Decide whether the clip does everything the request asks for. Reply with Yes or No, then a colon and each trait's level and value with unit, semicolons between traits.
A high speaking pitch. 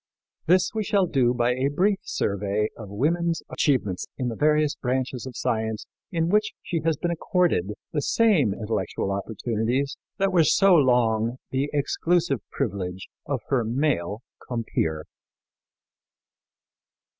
No: low, 130 Hz